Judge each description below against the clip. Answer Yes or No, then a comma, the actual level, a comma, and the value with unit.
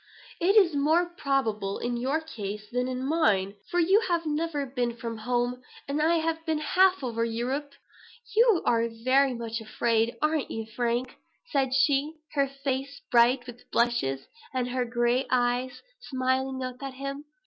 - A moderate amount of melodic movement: Yes, average, 4.0 semitones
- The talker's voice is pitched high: Yes, very high, 260 Hz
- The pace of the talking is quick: No, average, 165 wpm